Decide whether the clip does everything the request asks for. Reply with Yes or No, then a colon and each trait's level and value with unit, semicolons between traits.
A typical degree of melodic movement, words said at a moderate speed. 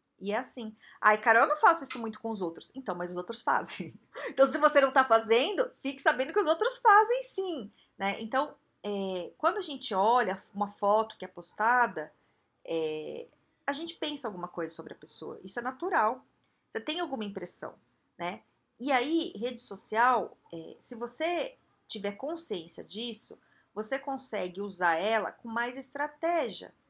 No: wide, 6.8 semitones; average, 170 wpm